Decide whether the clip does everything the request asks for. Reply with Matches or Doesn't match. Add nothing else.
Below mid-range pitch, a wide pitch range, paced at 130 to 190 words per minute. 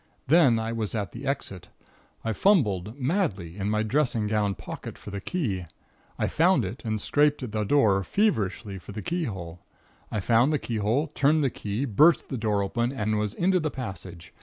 Matches